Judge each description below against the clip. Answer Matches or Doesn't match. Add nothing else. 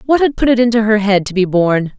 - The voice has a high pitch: Matches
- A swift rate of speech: Matches